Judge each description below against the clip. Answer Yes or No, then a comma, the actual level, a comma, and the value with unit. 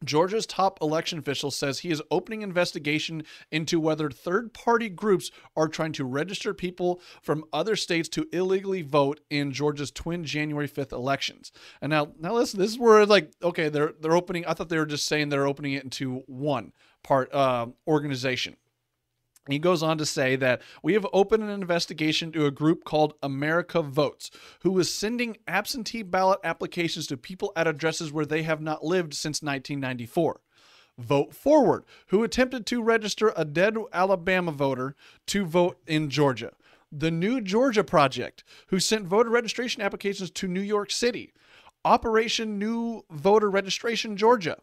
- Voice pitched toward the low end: No, medium, 170 Hz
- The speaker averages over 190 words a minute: No, average, 165 wpm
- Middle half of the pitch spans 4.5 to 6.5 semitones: Yes, wide, 5.4 semitones